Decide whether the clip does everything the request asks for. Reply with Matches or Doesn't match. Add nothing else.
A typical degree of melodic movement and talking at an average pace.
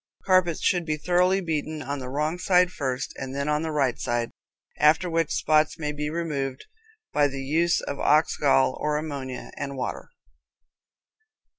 Matches